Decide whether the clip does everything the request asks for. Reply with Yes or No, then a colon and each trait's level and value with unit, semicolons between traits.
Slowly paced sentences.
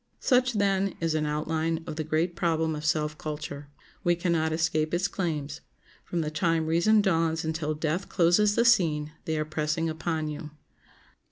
No: average, 175 wpm